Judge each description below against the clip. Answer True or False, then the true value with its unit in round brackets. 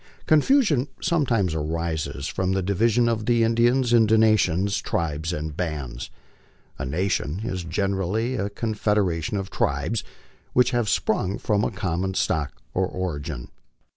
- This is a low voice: True (95 Hz)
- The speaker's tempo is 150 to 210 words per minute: False (135 wpm)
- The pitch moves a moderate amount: False (5.7 semitones)